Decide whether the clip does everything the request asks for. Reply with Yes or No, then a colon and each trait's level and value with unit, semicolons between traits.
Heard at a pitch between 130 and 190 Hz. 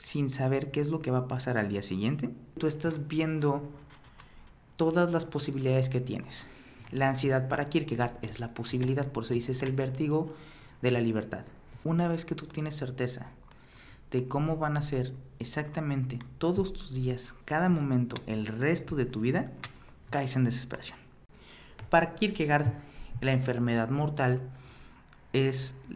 Yes: low, 135 Hz